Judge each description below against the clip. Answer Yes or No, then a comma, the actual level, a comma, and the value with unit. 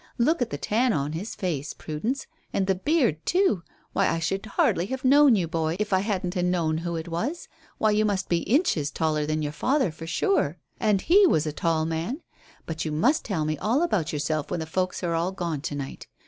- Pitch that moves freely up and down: Yes, wide, 5.9 semitones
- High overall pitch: No, medium, 180 Hz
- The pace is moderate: No, fast, 225 wpm